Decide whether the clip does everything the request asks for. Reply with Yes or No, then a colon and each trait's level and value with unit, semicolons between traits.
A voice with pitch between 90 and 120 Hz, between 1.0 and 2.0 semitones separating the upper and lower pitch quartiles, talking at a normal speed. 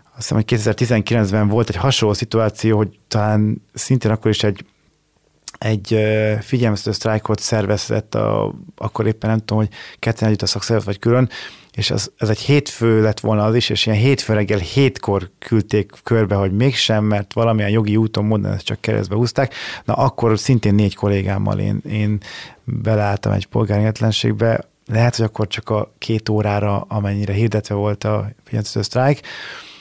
No: low, 110 Hz; narrow, 1.6 semitones; fast, 160 wpm